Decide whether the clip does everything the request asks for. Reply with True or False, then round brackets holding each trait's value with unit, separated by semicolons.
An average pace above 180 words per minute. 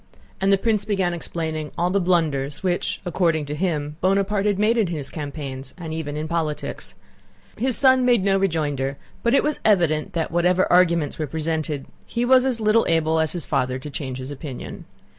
True (190 wpm)